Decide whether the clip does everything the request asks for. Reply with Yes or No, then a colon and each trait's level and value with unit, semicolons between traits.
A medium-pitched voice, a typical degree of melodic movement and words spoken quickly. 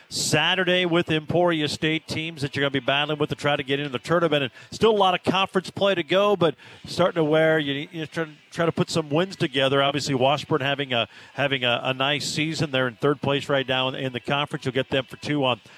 Yes: medium, 150 Hz; average, 3.1 semitones; fast, 245 wpm